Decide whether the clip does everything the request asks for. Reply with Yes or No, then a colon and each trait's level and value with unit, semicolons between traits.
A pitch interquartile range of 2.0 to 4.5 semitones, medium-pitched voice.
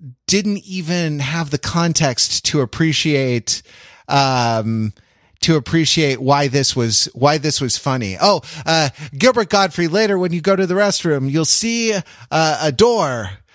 No: average, 5.0 semitones; medium, 150 Hz